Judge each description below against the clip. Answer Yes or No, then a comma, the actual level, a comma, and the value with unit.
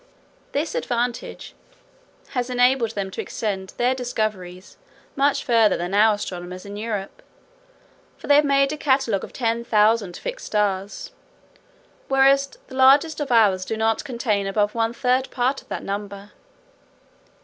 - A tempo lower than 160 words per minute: Yes, average, 145 wpm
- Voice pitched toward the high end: Yes, high, 230 Hz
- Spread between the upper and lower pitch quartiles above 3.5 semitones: Yes, average, 4.5 semitones